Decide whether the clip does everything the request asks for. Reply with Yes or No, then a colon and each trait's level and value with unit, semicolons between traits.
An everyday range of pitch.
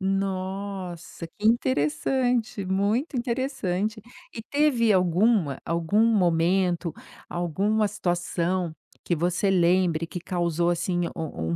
Yes: average, 3.8 semitones